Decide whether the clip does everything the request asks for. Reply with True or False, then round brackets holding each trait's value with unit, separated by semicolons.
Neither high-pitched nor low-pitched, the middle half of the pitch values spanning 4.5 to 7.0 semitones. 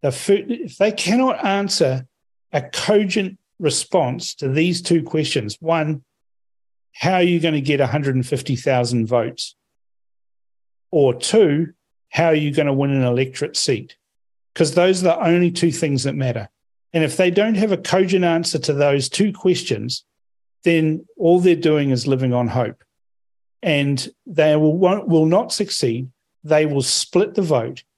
True (155 Hz; 5.5 semitones)